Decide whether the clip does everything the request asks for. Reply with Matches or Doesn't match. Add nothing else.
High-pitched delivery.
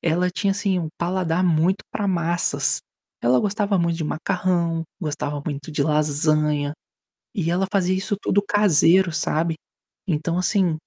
Doesn't match